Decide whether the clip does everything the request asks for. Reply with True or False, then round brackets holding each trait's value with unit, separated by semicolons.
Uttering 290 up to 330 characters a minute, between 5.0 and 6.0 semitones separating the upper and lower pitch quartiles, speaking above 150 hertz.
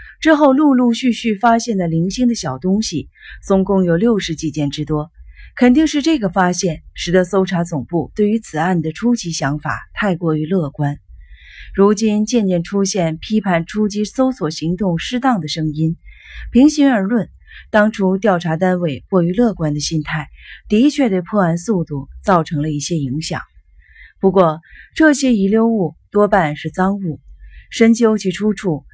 False (245 characters per minute; 5.5 semitones; 185 Hz)